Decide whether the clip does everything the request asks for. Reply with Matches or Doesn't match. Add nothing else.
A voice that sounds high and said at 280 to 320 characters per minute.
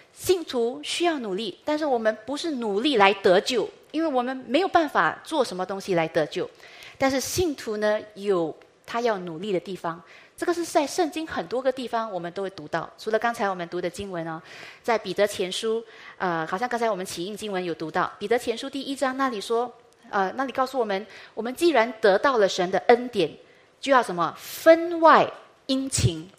Matches